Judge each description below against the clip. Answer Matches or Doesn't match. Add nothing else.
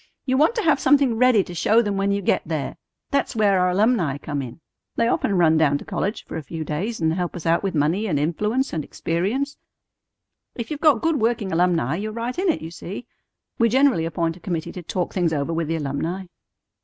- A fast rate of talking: Matches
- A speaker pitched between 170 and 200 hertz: Matches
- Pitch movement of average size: Doesn't match